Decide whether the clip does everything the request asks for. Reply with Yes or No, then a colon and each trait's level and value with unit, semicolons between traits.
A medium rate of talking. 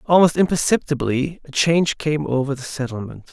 Yes: average, 145 wpm